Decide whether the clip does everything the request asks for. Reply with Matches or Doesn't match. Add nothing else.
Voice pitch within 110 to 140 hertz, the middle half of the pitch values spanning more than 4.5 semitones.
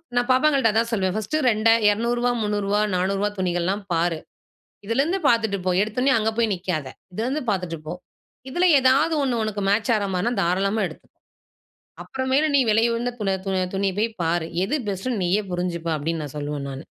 Doesn't match